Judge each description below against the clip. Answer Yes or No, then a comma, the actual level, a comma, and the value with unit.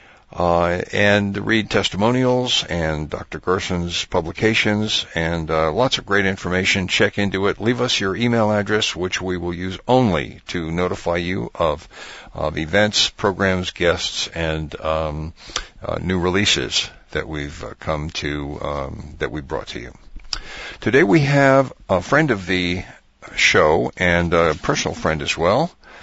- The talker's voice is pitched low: Yes, very low, 90 Hz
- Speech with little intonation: No, average, 3.6 semitones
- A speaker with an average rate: Yes, average, 150 wpm